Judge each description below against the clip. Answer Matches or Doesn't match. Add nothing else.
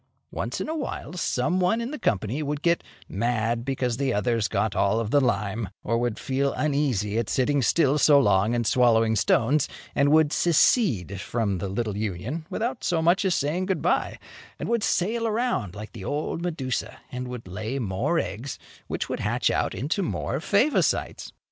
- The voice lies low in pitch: Matches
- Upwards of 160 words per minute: Matches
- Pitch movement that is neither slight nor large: Doesn't match